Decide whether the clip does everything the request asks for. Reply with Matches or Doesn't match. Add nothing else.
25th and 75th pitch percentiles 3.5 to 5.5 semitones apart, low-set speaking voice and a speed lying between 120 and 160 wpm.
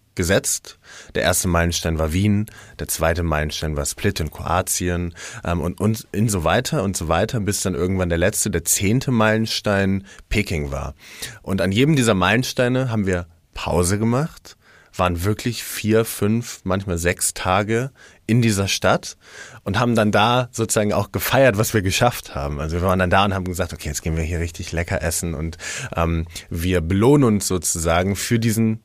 Doesn't match